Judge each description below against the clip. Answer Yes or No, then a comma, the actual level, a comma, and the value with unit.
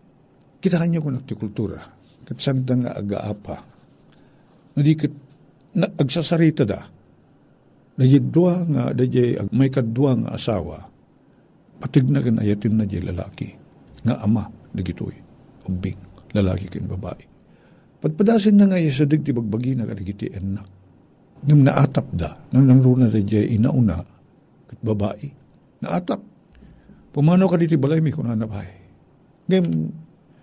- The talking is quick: No, average, 115 wpm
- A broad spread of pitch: Yes, wide, 6.2 semitones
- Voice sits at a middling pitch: No, low, 130 Hz